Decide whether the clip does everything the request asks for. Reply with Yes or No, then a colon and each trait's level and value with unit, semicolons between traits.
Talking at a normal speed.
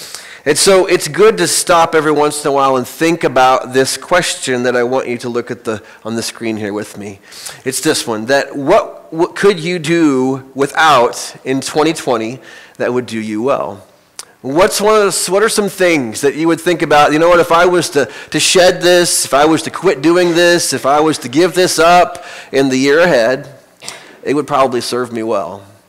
No: fast, 220 wpm